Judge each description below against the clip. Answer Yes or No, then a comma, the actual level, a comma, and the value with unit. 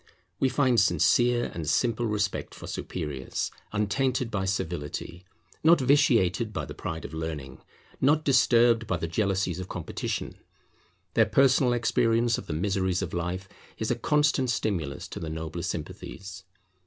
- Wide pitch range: Yes, wide, 5.9 semitones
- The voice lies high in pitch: No, low, 100 Hz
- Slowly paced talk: No, average, 145 wpm